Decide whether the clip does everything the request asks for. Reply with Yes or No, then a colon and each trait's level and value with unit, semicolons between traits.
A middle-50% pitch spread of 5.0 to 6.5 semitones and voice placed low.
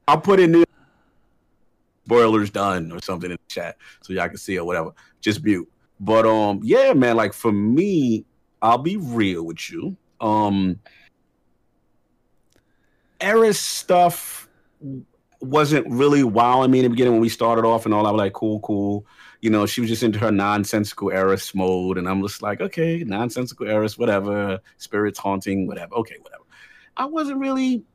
Yes: wide, 5.4 semitones; low, 110 Hz